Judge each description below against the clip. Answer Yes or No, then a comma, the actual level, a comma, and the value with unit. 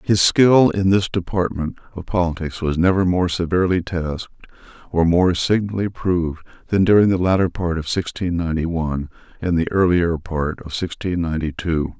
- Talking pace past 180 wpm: No, average, 165 wpm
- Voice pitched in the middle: No, very low, 85 Hz